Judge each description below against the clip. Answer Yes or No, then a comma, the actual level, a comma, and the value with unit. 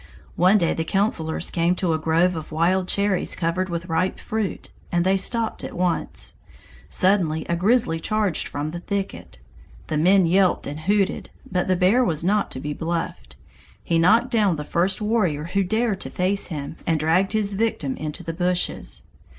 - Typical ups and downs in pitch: Yes, average, 3.4 semitones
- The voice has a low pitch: No, medium, 180 Hz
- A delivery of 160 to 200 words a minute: Yes, average, 180 wpm